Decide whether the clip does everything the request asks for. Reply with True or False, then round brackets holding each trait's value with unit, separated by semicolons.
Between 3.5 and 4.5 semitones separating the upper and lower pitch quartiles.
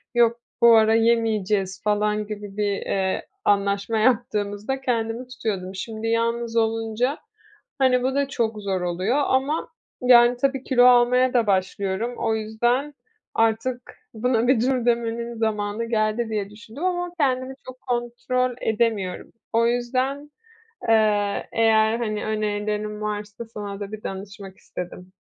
False (2.7 semitones)